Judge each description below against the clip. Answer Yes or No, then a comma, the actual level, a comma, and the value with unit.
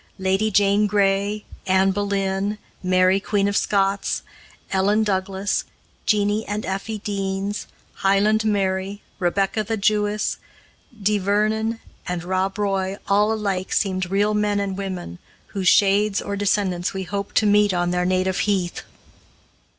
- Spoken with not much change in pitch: Yes, narrow, 1.6 semitones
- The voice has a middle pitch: No, high, 200 Hz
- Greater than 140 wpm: No, slow, 135 wpm